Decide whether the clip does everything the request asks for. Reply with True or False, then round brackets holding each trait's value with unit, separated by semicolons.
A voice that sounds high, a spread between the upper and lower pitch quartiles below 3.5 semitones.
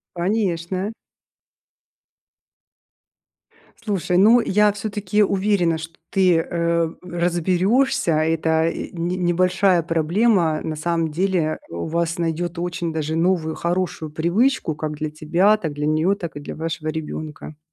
False (170 Hz; 2.9 semitones)